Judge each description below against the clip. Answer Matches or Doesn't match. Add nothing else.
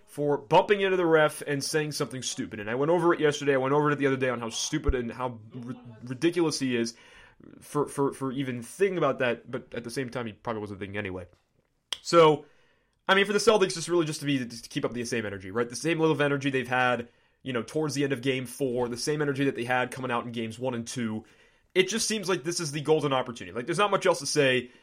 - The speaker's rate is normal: Doesn't match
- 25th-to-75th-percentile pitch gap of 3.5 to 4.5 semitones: Matches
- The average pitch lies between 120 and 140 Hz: Matches